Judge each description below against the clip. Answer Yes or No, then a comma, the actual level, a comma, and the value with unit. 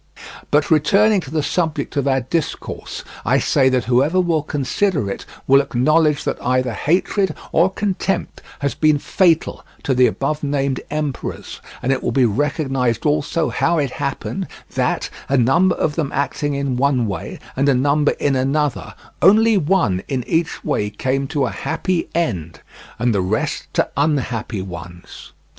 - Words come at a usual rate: Yes, average, 160 wpm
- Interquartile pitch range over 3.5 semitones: Yes, average, 3.9 semitones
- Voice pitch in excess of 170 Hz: No, medium, 140 Hz